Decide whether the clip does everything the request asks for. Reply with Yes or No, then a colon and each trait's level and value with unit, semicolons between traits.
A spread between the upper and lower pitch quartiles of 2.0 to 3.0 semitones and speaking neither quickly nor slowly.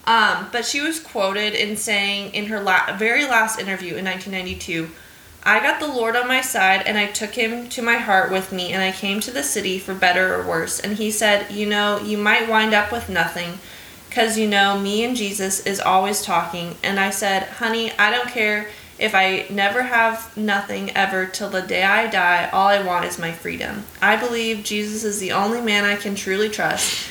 No: narrow, 2.6 semitones; fast, 215 wpm